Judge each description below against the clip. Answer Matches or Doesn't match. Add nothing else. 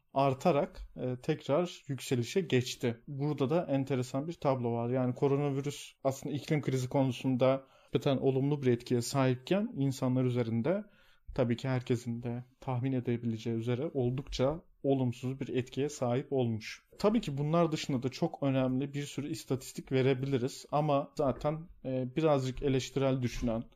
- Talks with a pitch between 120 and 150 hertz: Matches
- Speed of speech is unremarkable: Matches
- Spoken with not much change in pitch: Matches